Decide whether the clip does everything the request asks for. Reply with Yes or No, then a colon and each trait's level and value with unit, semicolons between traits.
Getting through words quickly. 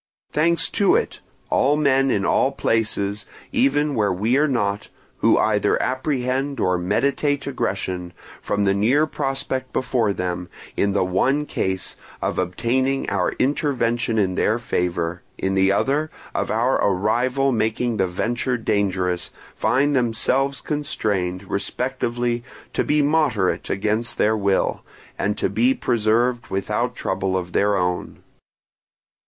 No: slow, 135 wpm